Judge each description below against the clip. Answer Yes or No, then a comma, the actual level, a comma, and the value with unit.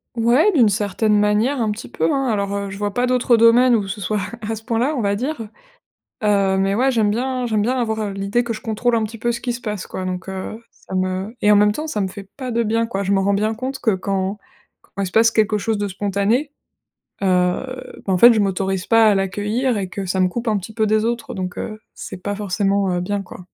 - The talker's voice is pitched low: No, high, 210 Hz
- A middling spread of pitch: Yes, average, 3.0 semitones